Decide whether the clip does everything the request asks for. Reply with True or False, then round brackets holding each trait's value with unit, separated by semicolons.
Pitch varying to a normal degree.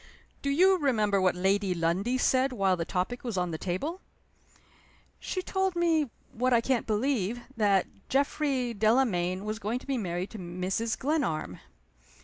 False (6.3 semitones)